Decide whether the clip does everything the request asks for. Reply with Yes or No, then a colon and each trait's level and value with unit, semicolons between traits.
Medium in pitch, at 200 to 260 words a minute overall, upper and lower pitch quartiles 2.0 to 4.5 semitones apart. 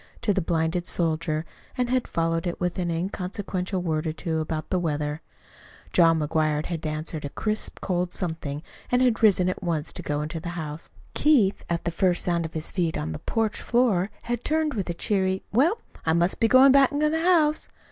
No: medium, 175 Hz; fast, 205 wpm; average, 5.1 semitones